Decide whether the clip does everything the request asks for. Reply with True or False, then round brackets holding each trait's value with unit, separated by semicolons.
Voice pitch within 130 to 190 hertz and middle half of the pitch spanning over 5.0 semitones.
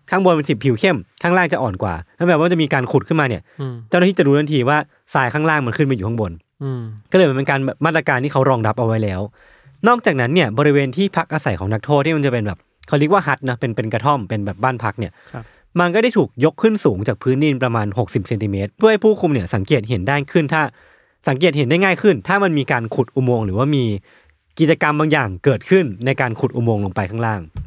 True (135 Hz; 5.6 semitones)